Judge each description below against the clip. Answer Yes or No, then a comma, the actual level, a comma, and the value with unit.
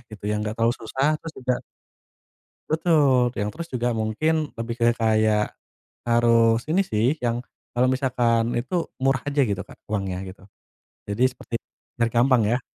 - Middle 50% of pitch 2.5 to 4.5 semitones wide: Yes, average, 3.3 semitones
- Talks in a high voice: No, low, 120 Hz